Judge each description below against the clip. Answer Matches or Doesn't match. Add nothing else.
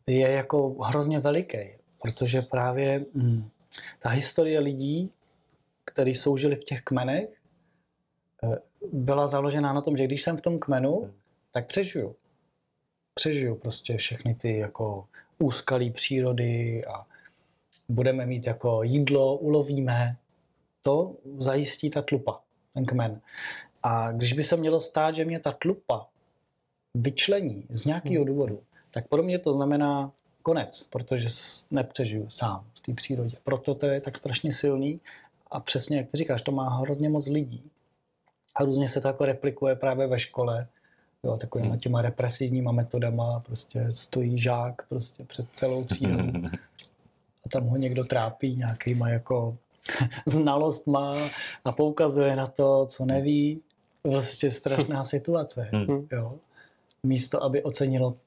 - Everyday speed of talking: Matches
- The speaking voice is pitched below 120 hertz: Doesn't match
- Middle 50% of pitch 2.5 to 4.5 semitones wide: Matches